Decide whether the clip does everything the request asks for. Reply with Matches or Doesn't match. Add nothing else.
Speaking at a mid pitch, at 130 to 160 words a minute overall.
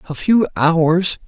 Matches